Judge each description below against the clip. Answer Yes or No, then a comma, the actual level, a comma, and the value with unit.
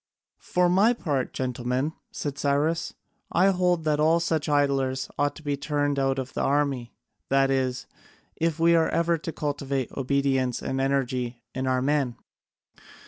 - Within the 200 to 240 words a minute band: No, average, 155 wpm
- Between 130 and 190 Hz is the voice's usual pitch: Yes, medium, 140 Hz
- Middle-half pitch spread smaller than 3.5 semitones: Yes, average, 3.1 semitones